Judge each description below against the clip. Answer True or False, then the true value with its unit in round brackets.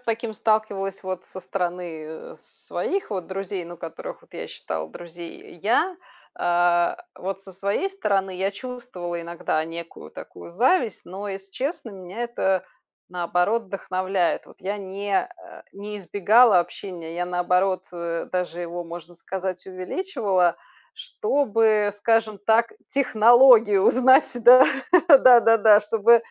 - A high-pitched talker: True (195 Hz)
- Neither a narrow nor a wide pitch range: True (4.2 semitones)